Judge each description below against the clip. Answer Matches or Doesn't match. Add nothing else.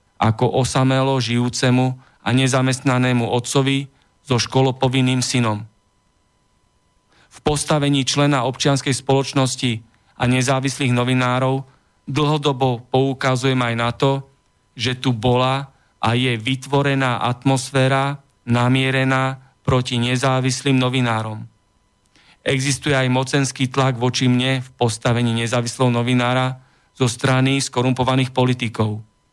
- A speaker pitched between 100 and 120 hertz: Doesn't match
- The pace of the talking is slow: Matches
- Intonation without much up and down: Matches